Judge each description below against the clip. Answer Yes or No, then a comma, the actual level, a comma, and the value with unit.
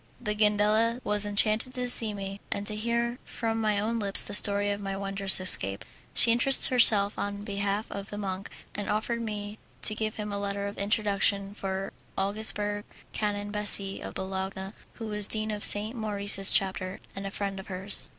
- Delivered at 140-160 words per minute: No, average, 185 wpm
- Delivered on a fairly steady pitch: Yes, narrow, 1.4 semitones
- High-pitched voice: Yes, high, 205 Hz